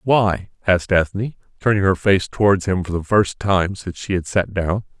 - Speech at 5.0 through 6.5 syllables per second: Yes, 5.1 syllables/s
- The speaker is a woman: No, male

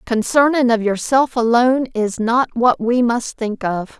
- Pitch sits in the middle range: No, high, 235 Hz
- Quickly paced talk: No, average, 165 wpm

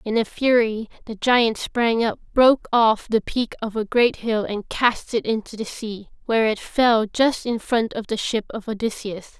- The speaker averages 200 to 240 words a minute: Yes, fast, 205 wpm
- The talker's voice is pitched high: Yes, high, 225 Hz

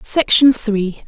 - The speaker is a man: No, female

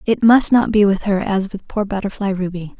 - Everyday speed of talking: No, fast, 235 wpm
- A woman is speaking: Yes, female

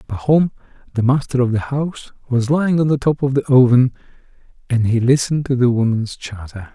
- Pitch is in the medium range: No, low, 130 Hz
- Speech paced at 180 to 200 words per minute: Yes, average, 185 wpm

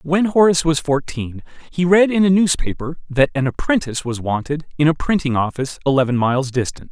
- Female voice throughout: No, male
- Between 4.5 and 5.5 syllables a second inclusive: No, 5.9 syllables/s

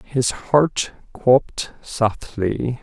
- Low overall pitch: Yes, low, 125 Hz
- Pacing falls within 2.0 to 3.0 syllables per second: Yes, 2.4 syllables/s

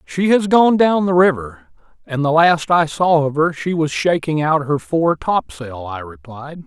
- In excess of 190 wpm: Yes, average, 200 wpm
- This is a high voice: No, medium, 150 Hz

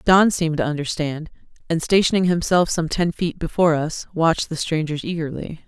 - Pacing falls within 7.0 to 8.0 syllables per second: No, 5.5 syllables/s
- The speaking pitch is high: No, medium, 165 Hz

